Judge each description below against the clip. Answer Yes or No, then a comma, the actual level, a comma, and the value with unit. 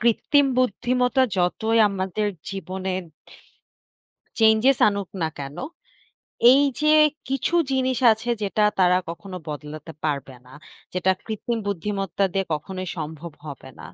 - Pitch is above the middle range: Yes, high, 195 Hz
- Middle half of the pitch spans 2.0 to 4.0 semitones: No, wide, 5.5 semitones